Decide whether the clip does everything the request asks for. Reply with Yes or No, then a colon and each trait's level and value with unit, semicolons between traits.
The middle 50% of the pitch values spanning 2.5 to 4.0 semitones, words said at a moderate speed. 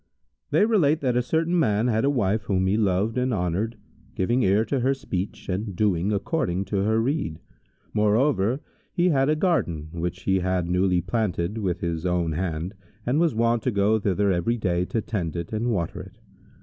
No: average, 5.2 semitones; average, 190 wpm